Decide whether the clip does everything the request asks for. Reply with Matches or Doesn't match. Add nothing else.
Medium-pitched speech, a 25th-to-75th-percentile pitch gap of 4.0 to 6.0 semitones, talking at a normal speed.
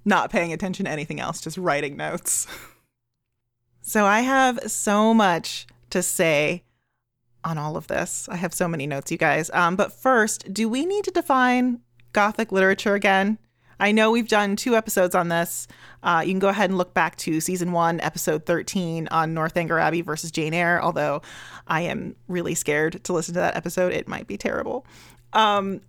Matches